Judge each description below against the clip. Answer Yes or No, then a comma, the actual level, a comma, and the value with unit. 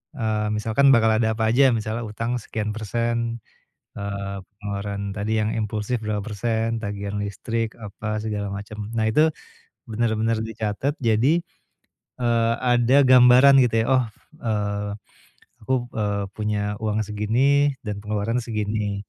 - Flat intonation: Yes, narrow, 2.0 semitones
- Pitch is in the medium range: No, low, 110 Hz